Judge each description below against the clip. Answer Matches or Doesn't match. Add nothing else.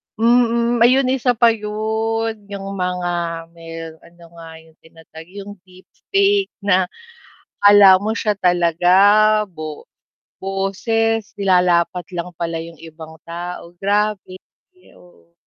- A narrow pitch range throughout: Doesn't match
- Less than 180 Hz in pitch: Doesn't match